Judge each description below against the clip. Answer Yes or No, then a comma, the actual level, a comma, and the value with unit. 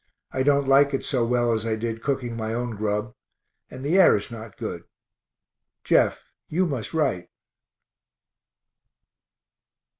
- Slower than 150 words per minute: Yes, average, 140 wpm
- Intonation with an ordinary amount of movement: Yes, average, 3.8 semitones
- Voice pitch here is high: No, low, 120 Hz